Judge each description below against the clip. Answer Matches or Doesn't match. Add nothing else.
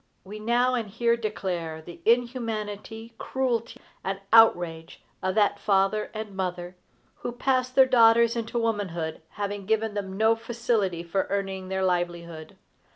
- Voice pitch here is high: Matches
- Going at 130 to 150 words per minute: Matches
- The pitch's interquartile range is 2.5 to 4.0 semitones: Matches